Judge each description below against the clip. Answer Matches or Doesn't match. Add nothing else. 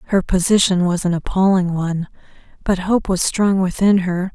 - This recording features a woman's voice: Matches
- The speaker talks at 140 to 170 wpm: Matches